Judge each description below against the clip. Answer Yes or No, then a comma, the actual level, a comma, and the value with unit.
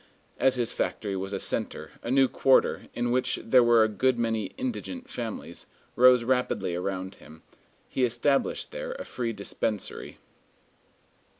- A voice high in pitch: No, low, 120 Hz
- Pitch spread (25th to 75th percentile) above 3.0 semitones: Yes, average, 3.7 semitones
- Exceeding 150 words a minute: No, average, 145 wpm